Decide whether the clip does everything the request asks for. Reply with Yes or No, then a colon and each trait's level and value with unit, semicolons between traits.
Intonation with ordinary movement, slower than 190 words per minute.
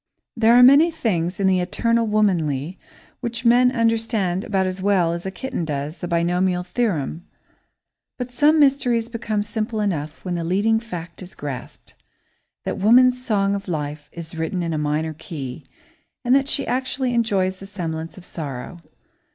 No: wide, 5.7 semitones; average, 165 wpm